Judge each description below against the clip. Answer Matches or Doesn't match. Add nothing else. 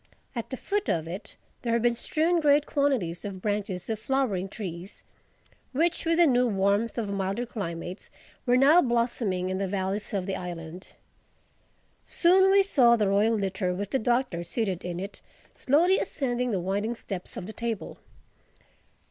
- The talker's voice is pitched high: Matches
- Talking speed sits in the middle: Matches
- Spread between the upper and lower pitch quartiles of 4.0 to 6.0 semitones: Matches